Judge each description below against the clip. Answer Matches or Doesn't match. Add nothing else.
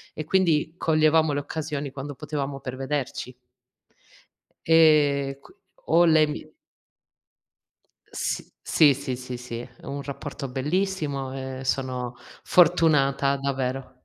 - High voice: Doesn't match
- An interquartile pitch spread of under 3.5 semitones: Matches